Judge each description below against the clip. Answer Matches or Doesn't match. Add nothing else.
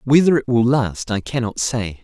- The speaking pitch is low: Matches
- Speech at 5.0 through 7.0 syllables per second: Doesn't match